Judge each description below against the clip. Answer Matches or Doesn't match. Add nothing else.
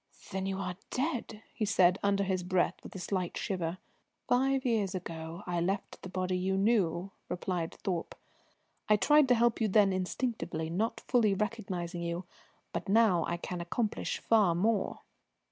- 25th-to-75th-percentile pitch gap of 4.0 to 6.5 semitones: Doesn't match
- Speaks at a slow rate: Doesn't match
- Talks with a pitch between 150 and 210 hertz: Matches